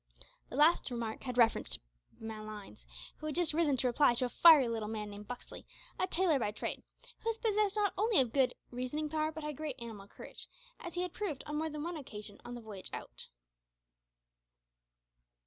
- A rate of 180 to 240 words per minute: Yes, average, 195 wpm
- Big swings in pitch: Yes, wide, 6.1 semitones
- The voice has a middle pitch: No, very high, 270 Hz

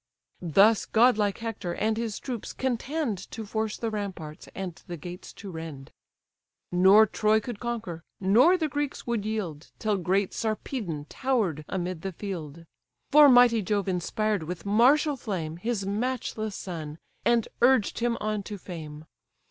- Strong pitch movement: No, average, 4.7 semitones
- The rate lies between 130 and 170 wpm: Yes, average, 150 wpm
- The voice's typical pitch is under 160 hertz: No, high, 210 Hz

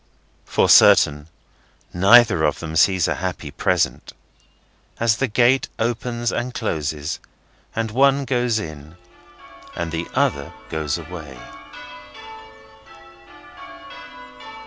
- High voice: No, very low, 90 Hz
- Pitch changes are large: Yes, wide, 7.3 semitones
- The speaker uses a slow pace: Yes, slow, 100 wpm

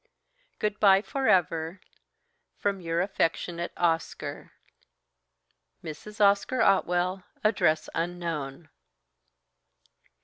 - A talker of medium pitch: Yes, medium, 175 Hz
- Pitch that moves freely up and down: No, average, 3.3 semitones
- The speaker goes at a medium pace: No, slow, 75 wpm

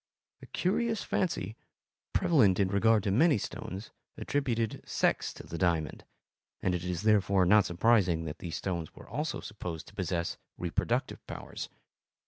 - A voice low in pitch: Yes, low, 100 Hz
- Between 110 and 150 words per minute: Yes, average, 145 wpm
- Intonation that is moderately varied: Yes, average, 4.4 semitones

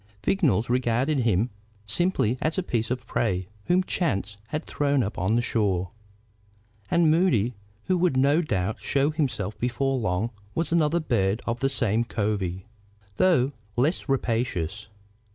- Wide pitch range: Yes, wide, 6.1 semitones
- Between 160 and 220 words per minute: No, average, 145 wpm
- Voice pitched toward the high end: No, low, 120 Hz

